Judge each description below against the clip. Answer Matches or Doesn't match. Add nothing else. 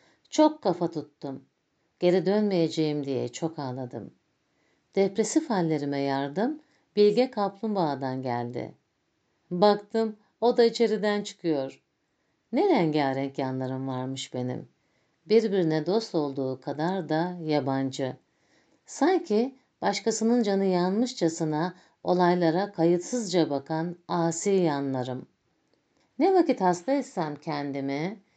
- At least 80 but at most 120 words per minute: Matches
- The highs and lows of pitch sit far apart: Matches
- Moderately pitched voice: Matches